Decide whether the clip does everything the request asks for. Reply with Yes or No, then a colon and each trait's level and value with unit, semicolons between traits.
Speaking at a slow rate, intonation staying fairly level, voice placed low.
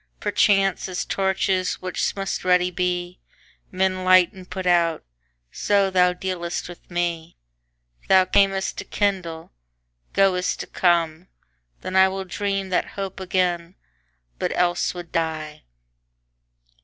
No: slow, 115 wpm; narrow, 1.8 semitones; medium, 180 Hz